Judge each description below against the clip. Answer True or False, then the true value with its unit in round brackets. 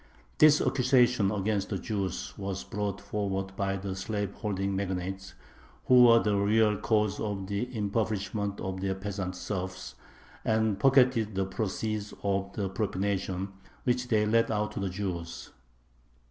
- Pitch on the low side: True (100 Hz)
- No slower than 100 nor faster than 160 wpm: True (140 wpm)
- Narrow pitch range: True (2.1 semitones)